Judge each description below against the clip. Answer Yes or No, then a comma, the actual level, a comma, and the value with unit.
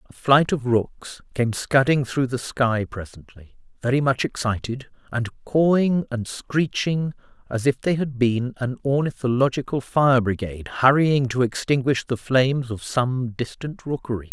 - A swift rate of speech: No, average, 145 wpm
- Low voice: Yes, low, 130 Hz